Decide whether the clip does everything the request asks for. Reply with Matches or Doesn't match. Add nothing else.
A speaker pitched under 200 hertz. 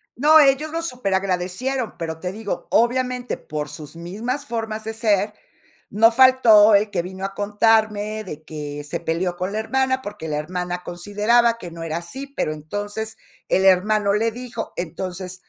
Doesn't match